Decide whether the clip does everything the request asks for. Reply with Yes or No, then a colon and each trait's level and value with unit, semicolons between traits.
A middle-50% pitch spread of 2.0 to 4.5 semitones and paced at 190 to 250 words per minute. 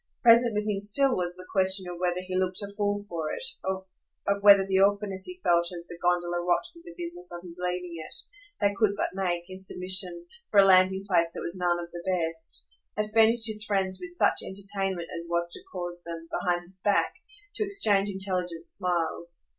Yes: narrow, 2.6 semitones; fast, 205 wpm